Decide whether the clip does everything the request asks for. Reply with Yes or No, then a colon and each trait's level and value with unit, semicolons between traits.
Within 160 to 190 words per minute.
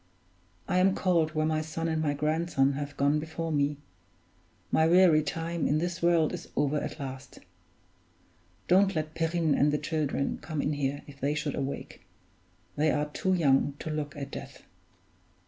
Yes: average, 170 wpm